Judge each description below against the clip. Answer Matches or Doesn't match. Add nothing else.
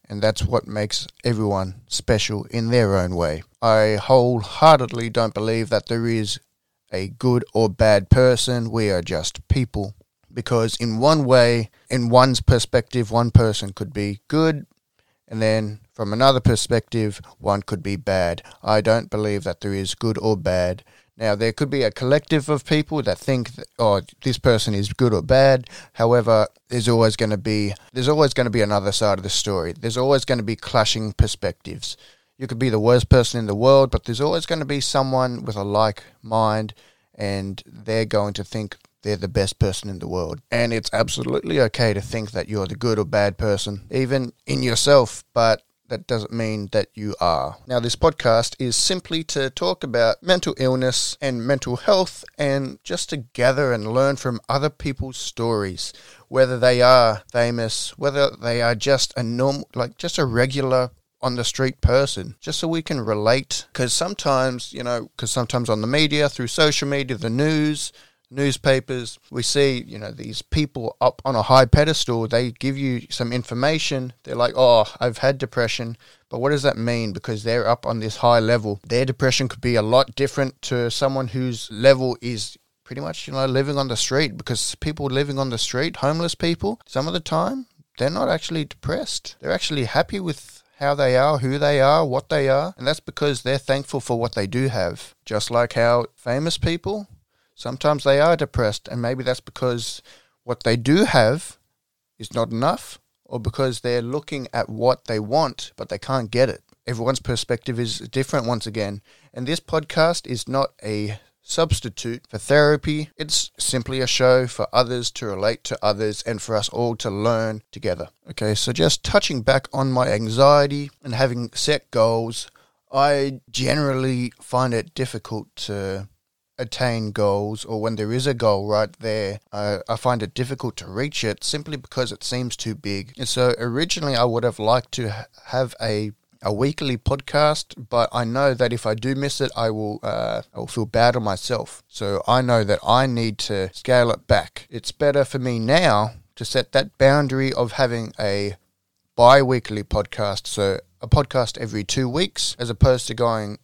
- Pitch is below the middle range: Matches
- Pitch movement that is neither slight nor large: Matches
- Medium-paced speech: Matches